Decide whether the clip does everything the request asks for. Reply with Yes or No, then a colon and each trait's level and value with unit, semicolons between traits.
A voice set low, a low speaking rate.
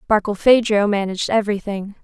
No: high, 205 Hz; slow, 90 wpm